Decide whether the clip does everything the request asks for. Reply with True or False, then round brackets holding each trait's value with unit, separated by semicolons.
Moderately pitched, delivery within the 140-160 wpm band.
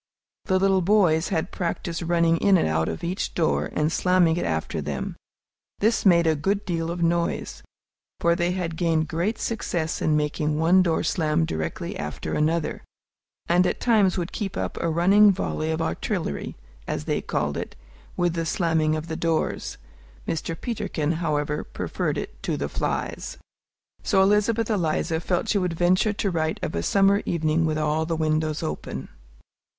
False (170 Hz; 170 wpm)